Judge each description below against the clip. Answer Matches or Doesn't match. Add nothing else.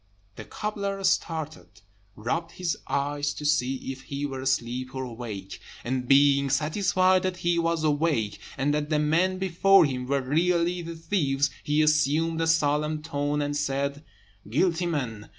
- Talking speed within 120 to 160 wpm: Matches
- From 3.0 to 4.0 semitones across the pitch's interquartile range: Matches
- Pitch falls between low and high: Matches